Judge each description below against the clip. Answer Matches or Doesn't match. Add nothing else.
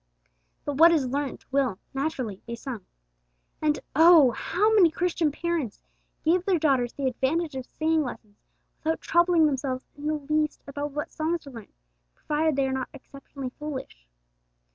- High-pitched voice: Matches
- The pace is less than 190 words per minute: Matches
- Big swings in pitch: Doesn't match